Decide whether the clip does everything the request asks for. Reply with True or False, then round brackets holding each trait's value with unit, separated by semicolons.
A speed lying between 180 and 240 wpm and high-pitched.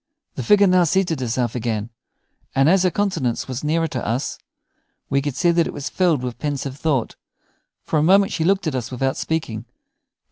False (190 wpm; 145 Hz)